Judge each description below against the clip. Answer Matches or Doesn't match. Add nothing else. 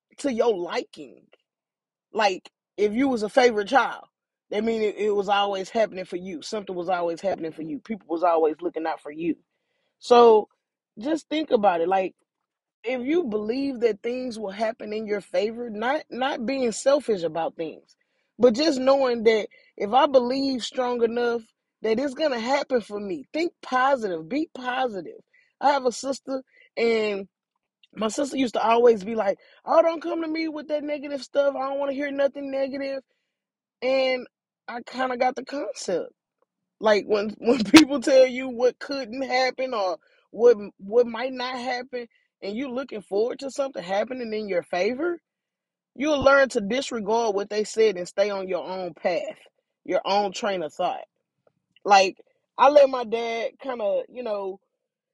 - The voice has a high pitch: Matches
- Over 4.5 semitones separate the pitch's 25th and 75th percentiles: Matches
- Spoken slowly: Doesn't match